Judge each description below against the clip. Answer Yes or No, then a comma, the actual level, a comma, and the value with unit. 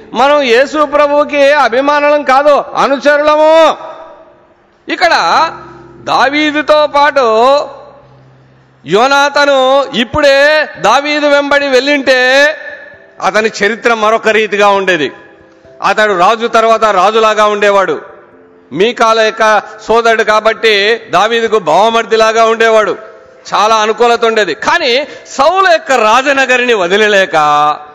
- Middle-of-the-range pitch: No, high, 245 Hz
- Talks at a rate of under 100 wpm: Yes, average, 85 wpm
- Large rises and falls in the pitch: No, average, 5.0 semitones